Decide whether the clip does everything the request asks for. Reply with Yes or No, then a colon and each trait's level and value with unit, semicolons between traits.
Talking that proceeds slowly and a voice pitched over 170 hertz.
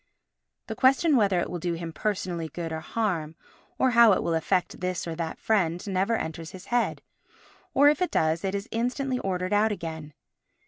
No: average, 190 wpm; medium, 185 Hz